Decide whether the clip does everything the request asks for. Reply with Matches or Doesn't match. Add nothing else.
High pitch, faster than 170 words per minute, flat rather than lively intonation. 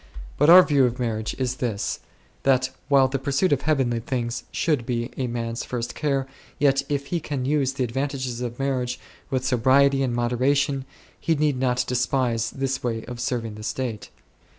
Doesn't match